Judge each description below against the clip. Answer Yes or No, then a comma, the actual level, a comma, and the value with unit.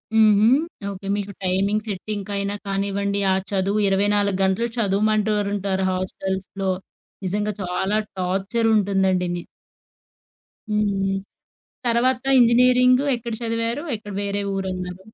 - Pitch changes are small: Yes, narrow, 2.0 semitones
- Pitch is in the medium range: No, high, 200 Hz